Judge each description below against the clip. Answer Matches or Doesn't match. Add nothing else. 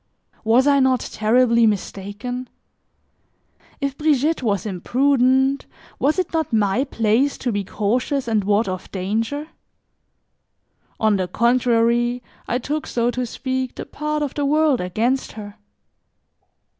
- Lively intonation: Doesn't match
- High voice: Matches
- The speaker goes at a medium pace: Doesn't match